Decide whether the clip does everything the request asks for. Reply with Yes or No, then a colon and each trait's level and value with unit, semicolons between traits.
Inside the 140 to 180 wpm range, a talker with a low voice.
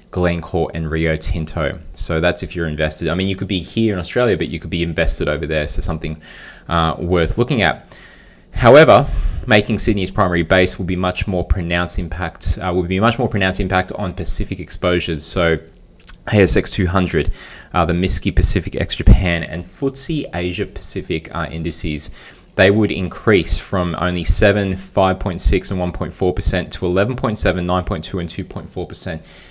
Yes: average, 165 wpm; very low, 90 Hz